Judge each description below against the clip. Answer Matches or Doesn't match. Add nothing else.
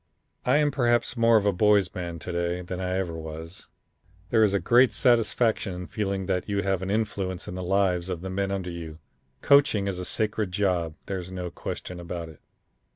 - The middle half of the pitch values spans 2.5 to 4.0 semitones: Matches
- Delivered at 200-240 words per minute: Matches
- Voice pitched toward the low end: Matches